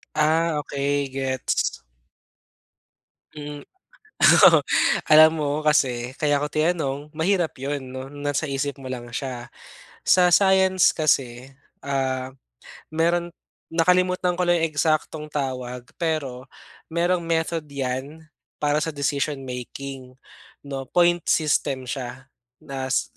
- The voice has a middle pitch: Yes, medium, 145 Hz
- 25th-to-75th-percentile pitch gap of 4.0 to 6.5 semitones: No, average, 3.5 semitones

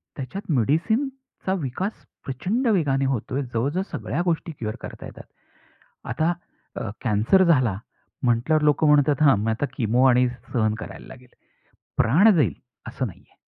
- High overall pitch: No, medium, 140 Hz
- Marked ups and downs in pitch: Yes, wide, 6.1 semitones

